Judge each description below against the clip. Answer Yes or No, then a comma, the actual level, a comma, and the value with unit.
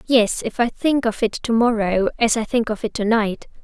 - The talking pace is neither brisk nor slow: No, fast, 245 wpm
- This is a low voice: No, high, 225 Hz